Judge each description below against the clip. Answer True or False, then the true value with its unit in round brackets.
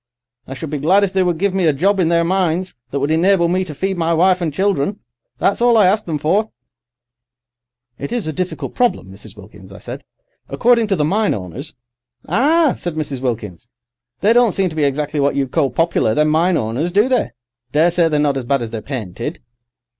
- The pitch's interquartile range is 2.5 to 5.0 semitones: False (5.5 semitones)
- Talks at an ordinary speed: False (215 wpm)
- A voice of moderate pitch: True (165 Hz)